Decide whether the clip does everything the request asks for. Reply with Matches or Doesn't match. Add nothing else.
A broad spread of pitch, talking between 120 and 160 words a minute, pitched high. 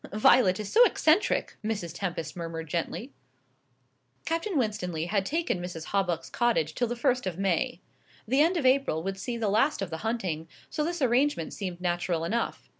Doesn't match